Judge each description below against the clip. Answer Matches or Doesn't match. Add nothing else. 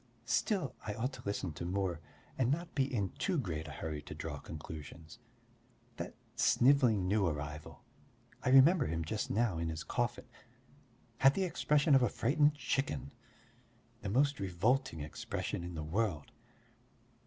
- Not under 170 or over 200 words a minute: Doesn't match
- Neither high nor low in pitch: Doesn't match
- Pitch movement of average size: Doesn't match